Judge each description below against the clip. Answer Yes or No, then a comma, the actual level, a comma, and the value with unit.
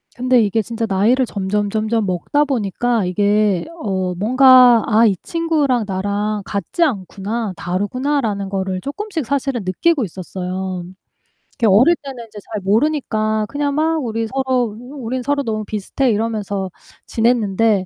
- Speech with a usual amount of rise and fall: Yes, average, 4.4 semitones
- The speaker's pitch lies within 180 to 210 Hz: No, high, 220 Hz